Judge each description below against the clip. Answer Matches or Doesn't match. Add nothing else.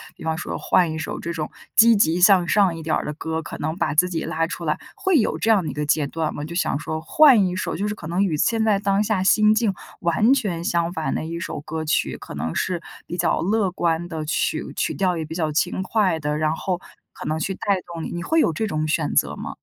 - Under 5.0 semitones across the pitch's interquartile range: Matches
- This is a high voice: Doesn't match